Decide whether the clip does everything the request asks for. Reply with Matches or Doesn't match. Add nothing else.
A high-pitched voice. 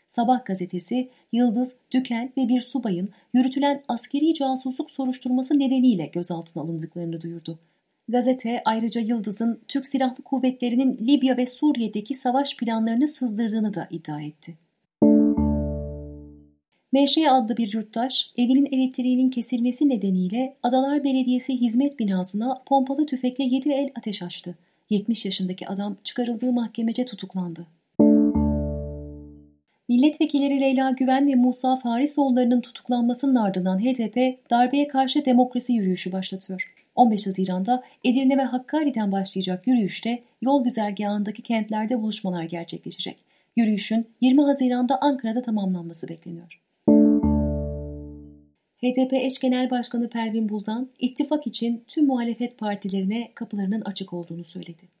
Matches